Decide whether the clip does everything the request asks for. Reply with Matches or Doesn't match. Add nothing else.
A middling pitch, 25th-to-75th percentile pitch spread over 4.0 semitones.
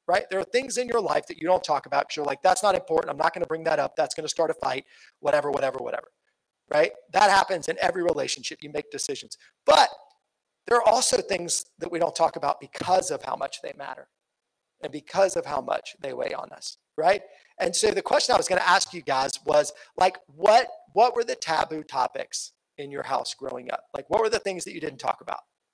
Matches